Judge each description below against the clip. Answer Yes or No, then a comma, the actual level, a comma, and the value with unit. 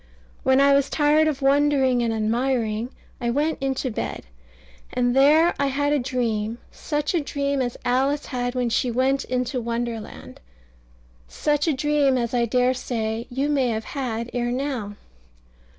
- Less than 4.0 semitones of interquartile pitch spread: Yes, average, 2.9 semitones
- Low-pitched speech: No, very high, 255 Hz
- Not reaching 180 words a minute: Yes, average, 160 wpm